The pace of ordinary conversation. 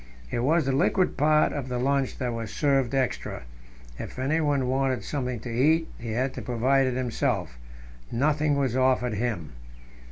Yes: average, 165 wpm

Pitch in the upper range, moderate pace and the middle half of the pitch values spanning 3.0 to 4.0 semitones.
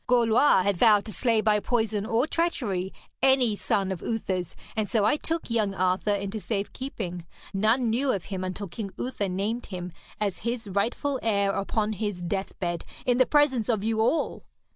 Yes: high, 215 Hz; average, 180 wpm; average, 3.4 semitones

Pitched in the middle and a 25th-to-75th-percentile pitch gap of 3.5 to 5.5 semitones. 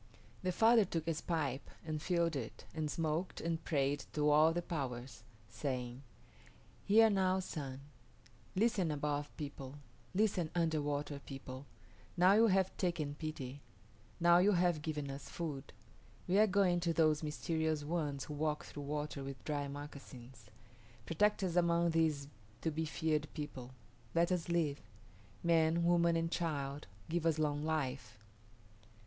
No: medium, 155 Hz; average, 3.1 semitones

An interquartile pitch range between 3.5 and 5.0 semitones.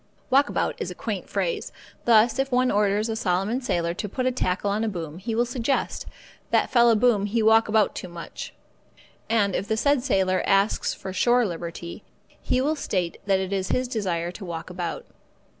Yes: average, 4.5 semitones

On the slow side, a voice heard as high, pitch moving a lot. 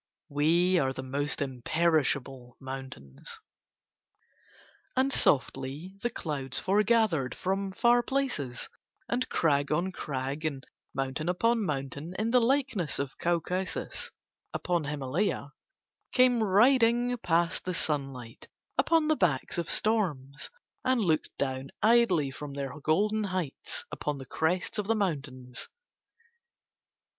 No: slow, 115 wpm; medium, 165 Hz; wide, 7.5 semitones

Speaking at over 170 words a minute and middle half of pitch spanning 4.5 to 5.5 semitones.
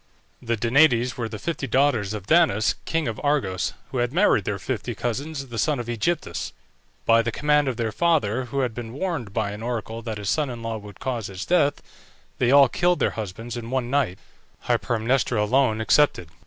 No: average, 195 wpm; average, 4.1 semitones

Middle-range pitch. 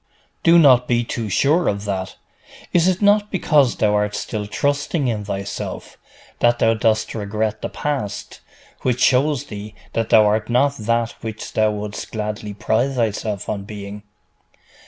No: low, 110 Hz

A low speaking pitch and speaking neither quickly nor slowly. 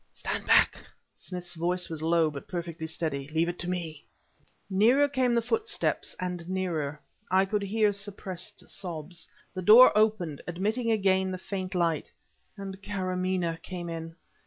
No: medium, 185 Hz; average, 150 wpm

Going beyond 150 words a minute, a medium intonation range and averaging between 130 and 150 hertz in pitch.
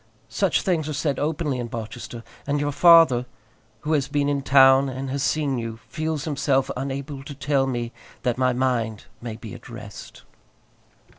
Yes: average, 170 wpm; average, 3.0 semitones; low, 135 Hz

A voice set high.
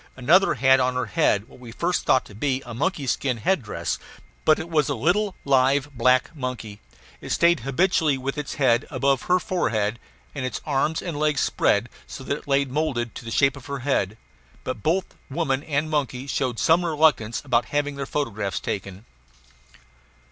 No: low, 135 Hz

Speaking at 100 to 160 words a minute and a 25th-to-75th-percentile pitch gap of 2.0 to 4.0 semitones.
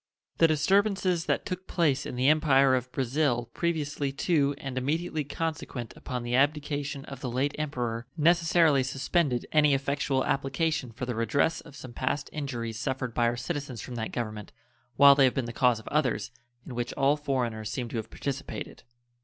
No: average, 180 wpm; average, 3.6 semitones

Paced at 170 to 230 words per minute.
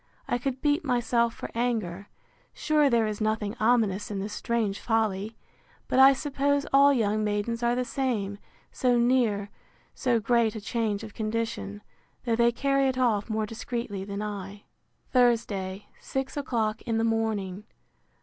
No: average, 150 wpm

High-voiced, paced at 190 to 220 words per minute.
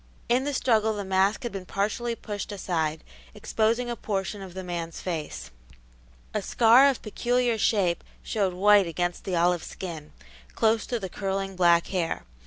No: high, 195 Hz; average, 165 wpm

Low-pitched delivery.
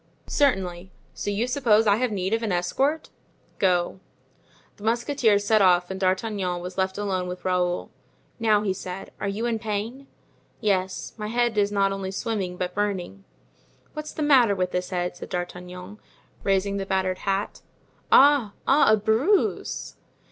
No: high, 200 Hz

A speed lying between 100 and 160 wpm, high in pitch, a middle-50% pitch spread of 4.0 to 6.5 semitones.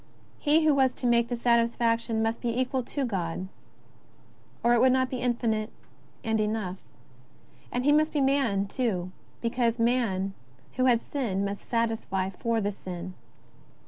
No: average, 150 wpm; high, 230 Hz; average, 3.6 semitones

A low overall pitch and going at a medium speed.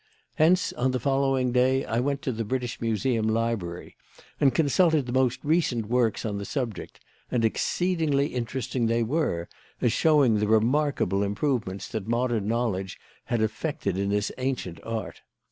Yes: low, 120 Hz; average, 155 wpm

